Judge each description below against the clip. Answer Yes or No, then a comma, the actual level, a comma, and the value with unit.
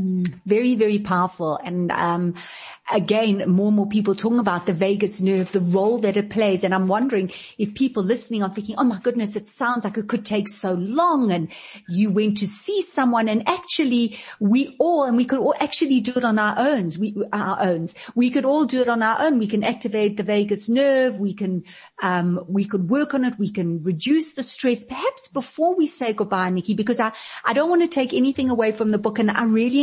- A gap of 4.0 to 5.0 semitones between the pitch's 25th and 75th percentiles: Yes, average, 4.3 semitones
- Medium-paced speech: No, fast, 220 wpm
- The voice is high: Yes, high, 215 Hz